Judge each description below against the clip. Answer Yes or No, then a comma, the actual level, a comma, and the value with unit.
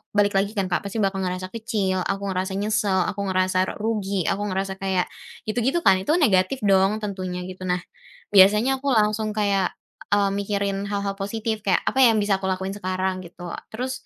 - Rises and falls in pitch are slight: Yes, narrow, 2.1 semitones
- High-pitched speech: Yes, high, 195 Hz